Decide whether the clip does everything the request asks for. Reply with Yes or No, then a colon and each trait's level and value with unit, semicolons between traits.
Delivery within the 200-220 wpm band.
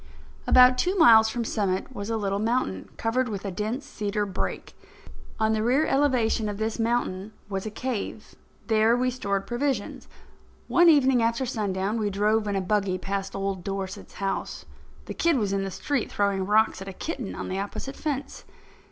No: average, 180 wpm